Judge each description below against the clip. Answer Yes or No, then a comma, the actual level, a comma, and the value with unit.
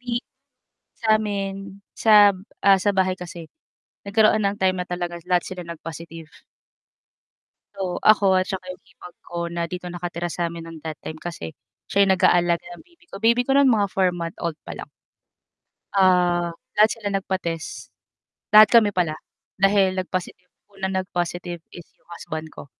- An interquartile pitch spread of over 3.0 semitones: No, narrow, 2.5 semitones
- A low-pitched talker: No, medium, 185 Hz